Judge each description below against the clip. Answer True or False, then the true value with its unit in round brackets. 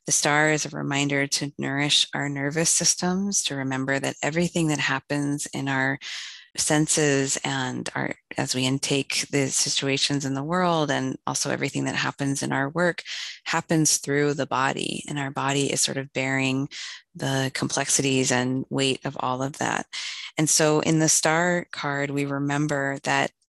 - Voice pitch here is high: False (140 Hz)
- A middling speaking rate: True (165 wpm)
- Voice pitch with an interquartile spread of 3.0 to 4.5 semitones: False (2.4 semitones)